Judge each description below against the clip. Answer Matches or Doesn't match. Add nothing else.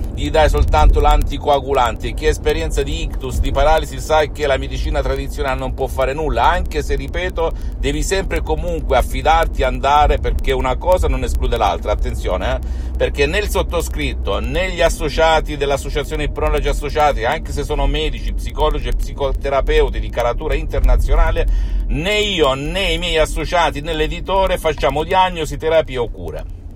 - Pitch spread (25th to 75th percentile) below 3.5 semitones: Doesn't match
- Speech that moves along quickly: Doesn't match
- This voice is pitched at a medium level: Matches